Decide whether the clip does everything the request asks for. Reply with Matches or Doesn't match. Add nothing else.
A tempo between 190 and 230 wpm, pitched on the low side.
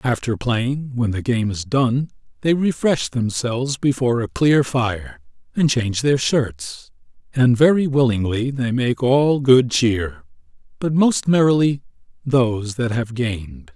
Doesn't match